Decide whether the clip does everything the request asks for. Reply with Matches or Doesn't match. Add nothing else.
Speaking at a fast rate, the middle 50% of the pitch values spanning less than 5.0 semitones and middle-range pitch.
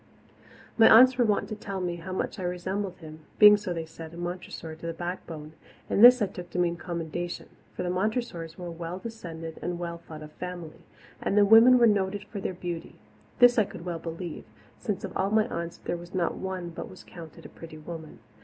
Matches